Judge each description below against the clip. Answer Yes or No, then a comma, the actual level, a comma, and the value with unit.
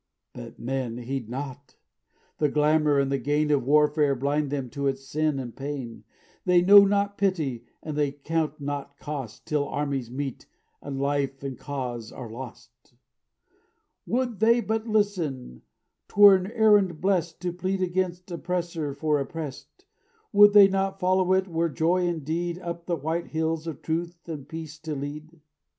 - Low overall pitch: No, medium, 155 Hz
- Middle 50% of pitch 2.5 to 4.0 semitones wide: No, average, 4.5 semitones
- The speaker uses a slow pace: No, average, 160 wpm